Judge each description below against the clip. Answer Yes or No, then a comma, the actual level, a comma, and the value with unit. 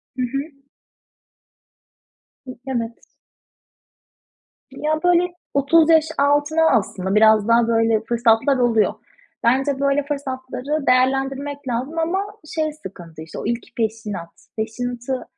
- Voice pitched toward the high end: Yes, very high, 260 Hz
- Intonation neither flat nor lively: Yes, average, 4.3 semitones